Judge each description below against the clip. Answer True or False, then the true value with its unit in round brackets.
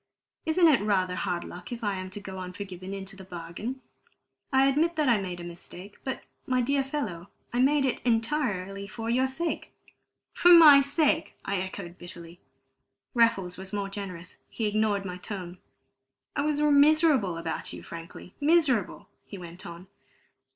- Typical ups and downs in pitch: False (6.9 semitones)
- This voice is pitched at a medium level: False (205 Hz)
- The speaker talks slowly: False (165 wpm)